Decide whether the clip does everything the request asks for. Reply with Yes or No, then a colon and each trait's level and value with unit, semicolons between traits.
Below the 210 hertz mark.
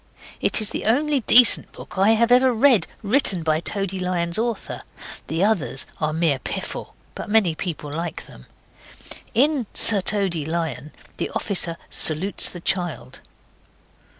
Yes: high, 190 Hz